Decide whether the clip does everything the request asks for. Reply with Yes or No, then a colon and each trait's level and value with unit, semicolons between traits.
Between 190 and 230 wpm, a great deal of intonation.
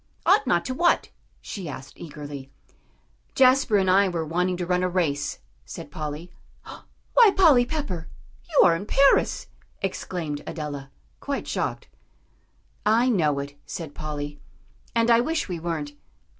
No: average, 145 wpm; wide, 7.5 semitones